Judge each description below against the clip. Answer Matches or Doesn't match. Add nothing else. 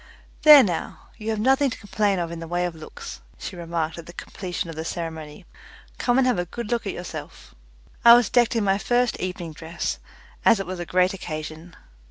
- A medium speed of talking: Doesn't match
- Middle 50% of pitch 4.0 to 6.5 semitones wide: Matches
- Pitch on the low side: Doesn't match